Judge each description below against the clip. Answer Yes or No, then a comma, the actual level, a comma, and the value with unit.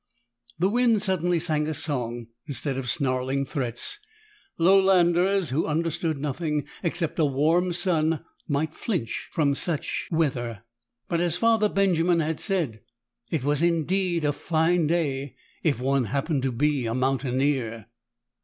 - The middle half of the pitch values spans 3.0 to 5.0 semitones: Yes, average, 4.3 semitones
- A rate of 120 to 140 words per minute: Yes, slow, 135 wpm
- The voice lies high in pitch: No, medium, 155 Hz